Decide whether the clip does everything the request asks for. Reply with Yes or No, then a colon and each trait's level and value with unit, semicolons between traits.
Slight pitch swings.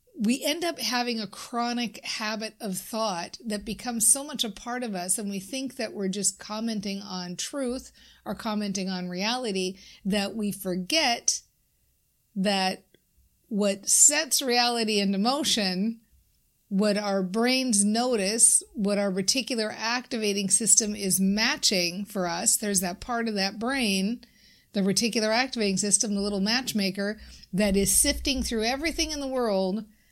No: average, 3.3 semitones